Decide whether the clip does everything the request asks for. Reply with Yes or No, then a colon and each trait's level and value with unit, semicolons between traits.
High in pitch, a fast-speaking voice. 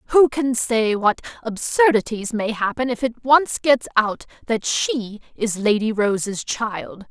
No: high, 235 Hz; average, 150 wpm